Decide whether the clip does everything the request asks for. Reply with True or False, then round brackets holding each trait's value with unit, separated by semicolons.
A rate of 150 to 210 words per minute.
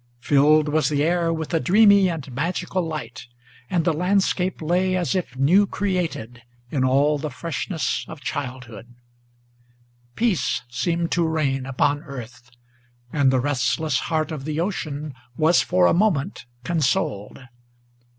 False (140 wpm)